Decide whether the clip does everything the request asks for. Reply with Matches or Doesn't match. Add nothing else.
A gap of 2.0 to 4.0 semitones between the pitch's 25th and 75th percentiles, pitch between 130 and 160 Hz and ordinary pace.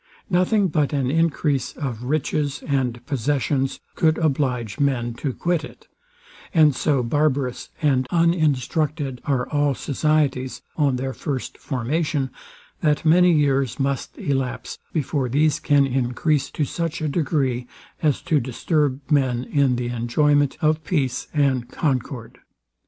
Doesn't match